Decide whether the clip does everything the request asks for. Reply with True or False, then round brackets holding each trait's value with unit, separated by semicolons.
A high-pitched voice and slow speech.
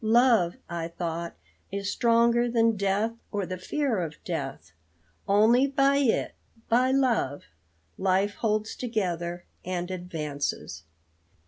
True (205 Hz; 115 wpm)